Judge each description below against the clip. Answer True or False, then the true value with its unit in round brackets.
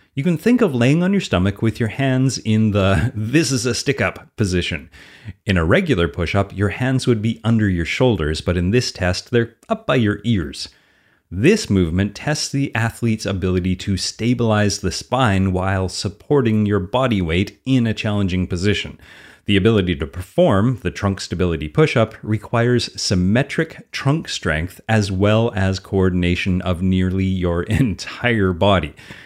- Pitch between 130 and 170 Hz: False (105 Hz)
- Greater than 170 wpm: False (165 wpm)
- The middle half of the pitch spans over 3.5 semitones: True (4.7 semitones)